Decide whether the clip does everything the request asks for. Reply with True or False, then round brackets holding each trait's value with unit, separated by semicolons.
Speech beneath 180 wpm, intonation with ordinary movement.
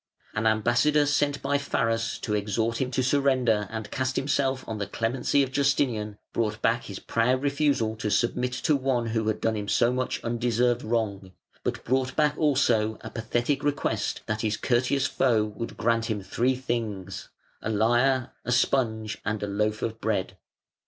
True (170 wpm; 3.3 semitones)